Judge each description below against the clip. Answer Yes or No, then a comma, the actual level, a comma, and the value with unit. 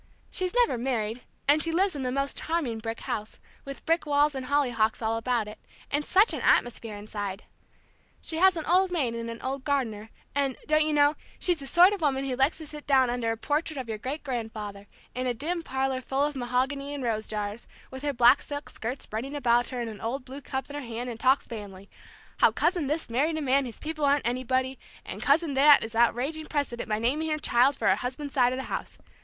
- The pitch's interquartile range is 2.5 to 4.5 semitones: Yes, average, 3.9 semitones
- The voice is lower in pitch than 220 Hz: No, very high, 265 Hz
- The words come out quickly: Yes, fast, 230 wpm